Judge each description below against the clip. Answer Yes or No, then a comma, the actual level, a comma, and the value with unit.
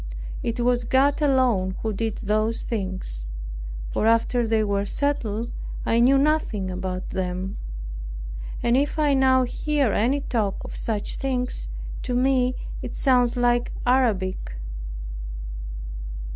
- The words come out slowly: Yes, slow, 125 wpm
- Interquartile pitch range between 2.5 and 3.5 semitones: No, average, 4.2 semitones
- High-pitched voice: Yes, high, 235 Hz